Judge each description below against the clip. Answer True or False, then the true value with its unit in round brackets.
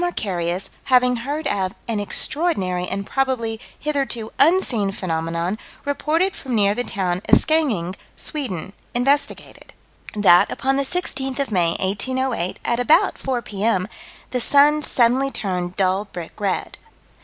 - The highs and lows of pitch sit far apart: True (6.3 semitones)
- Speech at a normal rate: False (130 wpm)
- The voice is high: True (230 Hz)